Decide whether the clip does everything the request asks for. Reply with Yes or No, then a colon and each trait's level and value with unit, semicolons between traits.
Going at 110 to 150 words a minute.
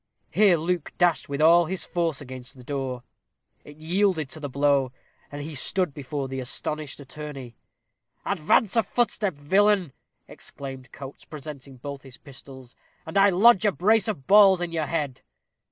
No: average, 160 wpm